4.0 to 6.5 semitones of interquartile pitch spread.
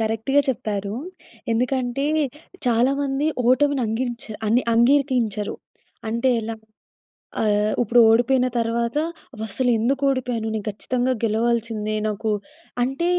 No: average, 2.7 semitones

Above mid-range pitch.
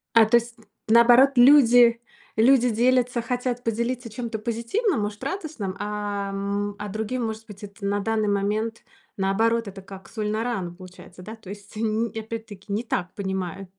Yes: high, 220 Hz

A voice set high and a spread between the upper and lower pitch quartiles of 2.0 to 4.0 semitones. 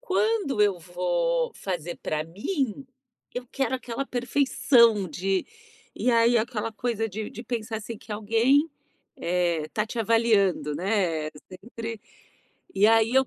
No: high, 225 Hz; average, 4.4 semitones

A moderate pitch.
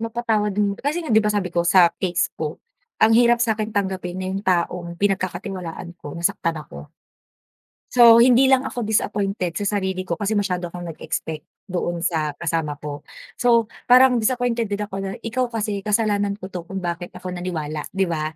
No: high, 195 Hz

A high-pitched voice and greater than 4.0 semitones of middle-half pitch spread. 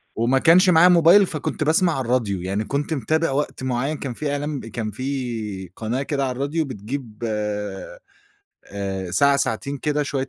No: low, 135 Hz; average, 4.8 semitones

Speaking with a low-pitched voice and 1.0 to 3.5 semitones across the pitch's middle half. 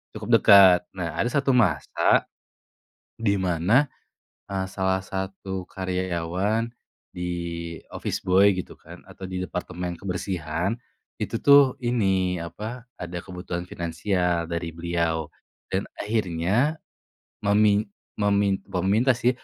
Yes: very low, 95 Hz; average, 2.9 semitones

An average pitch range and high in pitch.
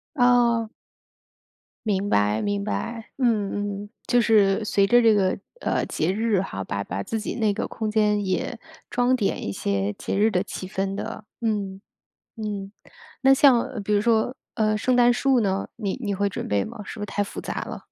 Yes: average, 3.1 semitones; high, 210 Hz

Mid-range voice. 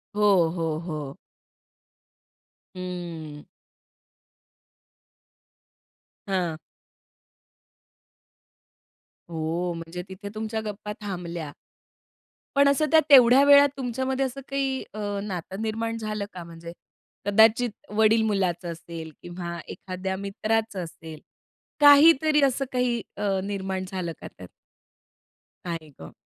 No: high, 195 Hz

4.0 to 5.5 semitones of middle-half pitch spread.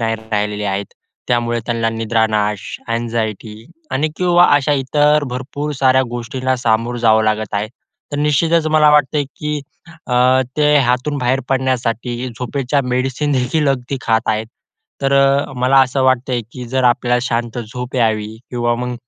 No: average, 3.0 semitones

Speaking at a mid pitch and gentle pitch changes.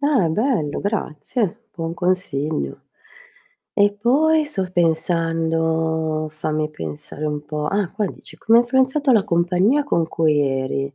No: medium, 170 Hz; wide, 5.9 semitones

